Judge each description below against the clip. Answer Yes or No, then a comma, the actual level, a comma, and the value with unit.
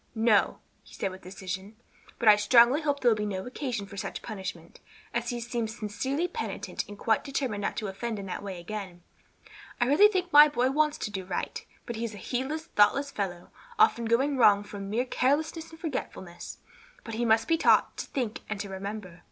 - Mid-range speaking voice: No, high, 225 Hz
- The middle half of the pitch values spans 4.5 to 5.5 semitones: Yes, average, 5.2 semitones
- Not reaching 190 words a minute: No, fast, 205 wpm